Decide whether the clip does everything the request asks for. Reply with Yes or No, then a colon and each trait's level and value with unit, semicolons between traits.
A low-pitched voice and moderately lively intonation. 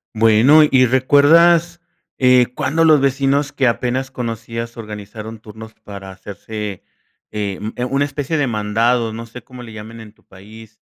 Yes: low, 115 Hz; average, 4.0 semitones